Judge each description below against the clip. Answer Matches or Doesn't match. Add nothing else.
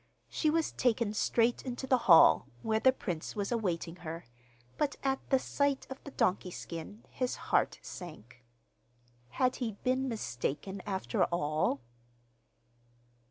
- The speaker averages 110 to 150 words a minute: Matches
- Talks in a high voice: Matches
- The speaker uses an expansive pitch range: Matches